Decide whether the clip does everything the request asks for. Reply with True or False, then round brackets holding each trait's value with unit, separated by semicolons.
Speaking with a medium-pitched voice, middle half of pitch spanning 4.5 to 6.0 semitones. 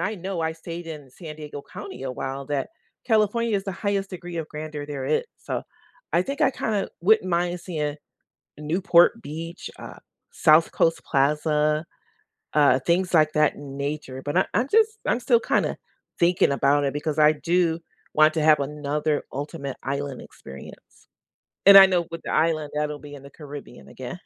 False (155 Hz; 3.5 semitones)